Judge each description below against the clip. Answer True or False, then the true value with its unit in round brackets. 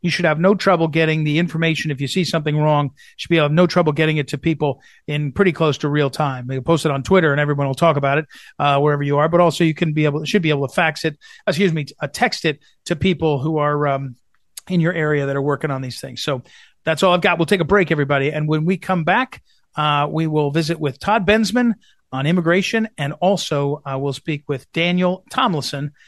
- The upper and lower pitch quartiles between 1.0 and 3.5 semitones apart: True (3.2 semitones)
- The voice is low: False (155 Hz)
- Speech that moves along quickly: True (255 wpm)